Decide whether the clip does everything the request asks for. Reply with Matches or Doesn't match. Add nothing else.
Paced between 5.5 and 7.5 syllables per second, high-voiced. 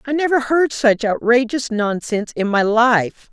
Doesn't match